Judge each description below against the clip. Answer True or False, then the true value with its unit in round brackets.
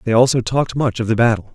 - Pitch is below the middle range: True (120 Hz)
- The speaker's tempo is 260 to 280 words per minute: True (270 wpm)